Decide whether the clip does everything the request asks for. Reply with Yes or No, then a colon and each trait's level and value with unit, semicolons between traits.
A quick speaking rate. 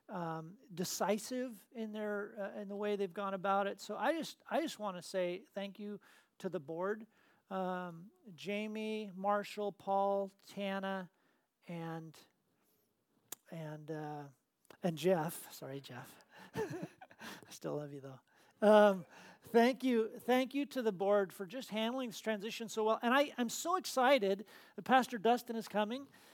No: average, 155 wpm